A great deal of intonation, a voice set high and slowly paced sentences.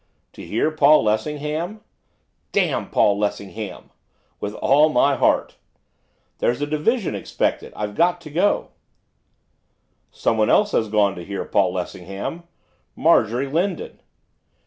No: wide, 7.5 semitones; medium, 140 Hz; slow, 120 wpm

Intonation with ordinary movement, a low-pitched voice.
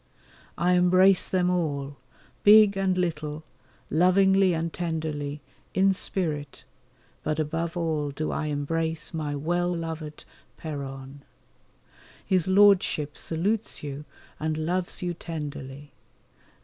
No: average, 3.4 semitones; medium, 160 Hz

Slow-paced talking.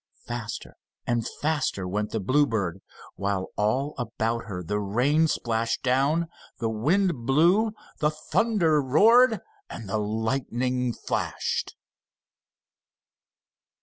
Yes: slow, 105 wpm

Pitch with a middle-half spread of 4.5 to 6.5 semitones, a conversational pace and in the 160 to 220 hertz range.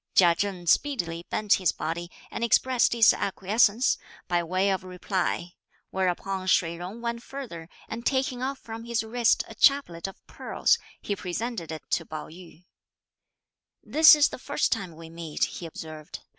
Yes: wide, 5.5 semitones; average, 160 wpm; high, 190 Hz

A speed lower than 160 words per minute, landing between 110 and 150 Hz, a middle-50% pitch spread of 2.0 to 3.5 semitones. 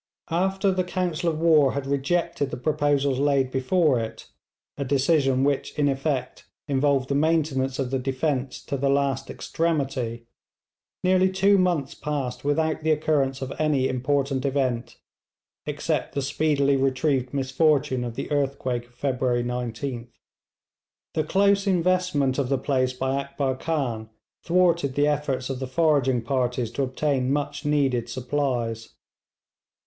Yes: average, 140 wpm; medium, 140 Hz; average, 2.9 semitones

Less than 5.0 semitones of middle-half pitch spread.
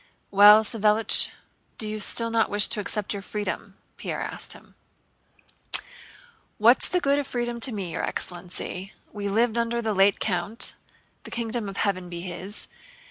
Yes: average, 2.8 semitones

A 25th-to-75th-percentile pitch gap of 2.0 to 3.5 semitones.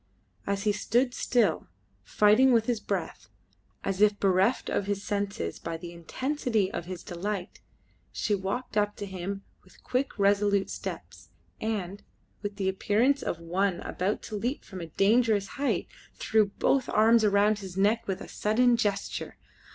Yes: narrow, 2.6 semitones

